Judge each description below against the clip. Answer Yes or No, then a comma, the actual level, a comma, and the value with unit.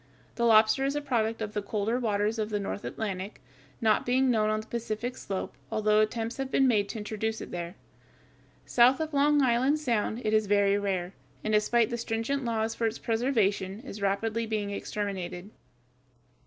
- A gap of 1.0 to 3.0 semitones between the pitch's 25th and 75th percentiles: Yes, narrow, 2.4 semitones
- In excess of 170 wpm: Yes, average, 180 wpm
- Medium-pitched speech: No, high, 220 Hz